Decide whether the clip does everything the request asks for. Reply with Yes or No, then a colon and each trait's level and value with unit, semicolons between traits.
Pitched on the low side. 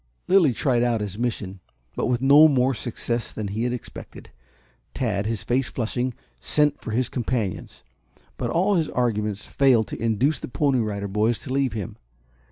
Yes: low, 120 Hz